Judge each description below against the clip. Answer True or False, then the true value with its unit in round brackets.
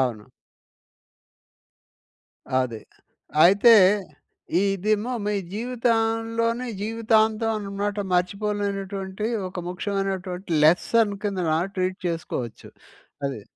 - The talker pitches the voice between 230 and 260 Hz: False (200 Hz)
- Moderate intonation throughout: True (3.4 semitones)